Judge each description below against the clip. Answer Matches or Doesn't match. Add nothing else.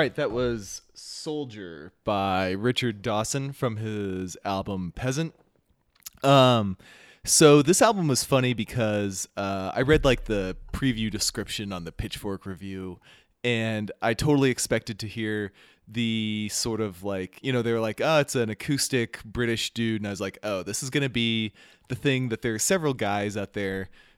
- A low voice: Matches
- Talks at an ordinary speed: Matches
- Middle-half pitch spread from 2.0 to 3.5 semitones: Doesn't match